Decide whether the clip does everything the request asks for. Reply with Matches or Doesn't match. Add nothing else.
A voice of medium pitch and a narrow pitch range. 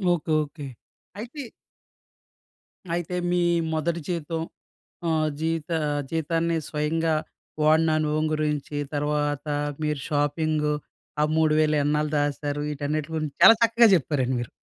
Matches